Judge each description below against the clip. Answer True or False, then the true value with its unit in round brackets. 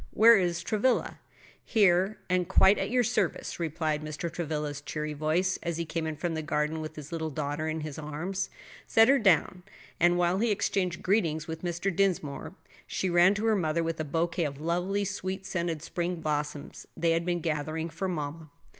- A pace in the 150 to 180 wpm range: False (190 wpm)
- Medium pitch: True (170 Hz)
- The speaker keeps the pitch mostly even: False (3.3 semitones)